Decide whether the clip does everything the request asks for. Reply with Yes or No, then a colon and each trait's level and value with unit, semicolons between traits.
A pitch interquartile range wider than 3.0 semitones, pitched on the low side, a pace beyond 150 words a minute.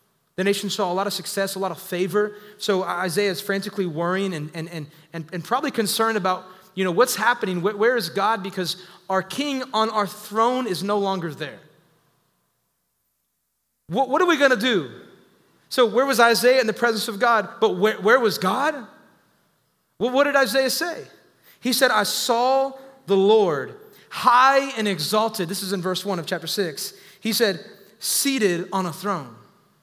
No: average, 4.3 semitones; high, 205 Hz; average, 180 wpm